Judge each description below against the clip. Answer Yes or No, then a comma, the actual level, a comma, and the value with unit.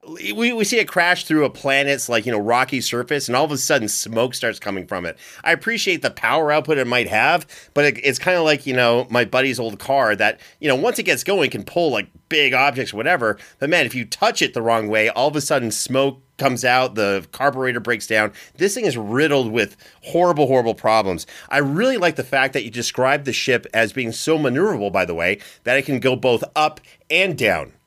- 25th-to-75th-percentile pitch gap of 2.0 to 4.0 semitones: No, average, 4.4 semitones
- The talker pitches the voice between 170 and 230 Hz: No, low, 135 Hz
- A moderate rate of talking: No, fast, 235 wpm